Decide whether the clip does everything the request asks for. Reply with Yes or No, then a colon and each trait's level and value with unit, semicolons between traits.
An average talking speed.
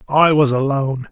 Yes: average, 160 wpm